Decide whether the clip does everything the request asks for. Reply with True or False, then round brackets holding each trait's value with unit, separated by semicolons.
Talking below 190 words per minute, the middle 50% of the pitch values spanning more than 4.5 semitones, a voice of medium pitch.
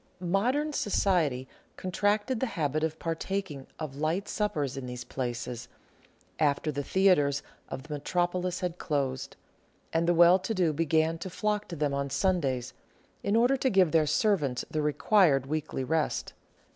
True (155 wpm; 5.2 semitones; 160 Hz)